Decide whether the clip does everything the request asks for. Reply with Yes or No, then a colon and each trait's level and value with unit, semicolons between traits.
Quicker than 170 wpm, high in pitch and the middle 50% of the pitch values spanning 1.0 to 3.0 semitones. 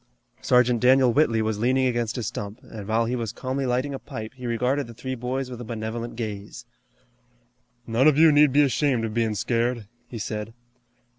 No: average, 195 wpm; low, 120 Hz; narrow, 2.6 semitones